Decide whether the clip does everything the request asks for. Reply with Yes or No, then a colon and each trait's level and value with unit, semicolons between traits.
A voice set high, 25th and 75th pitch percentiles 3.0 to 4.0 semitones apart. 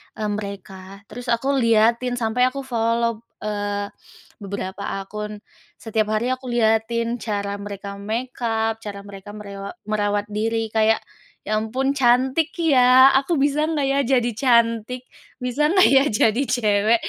Yes: high, 225 Hz; average, 3.4 semitones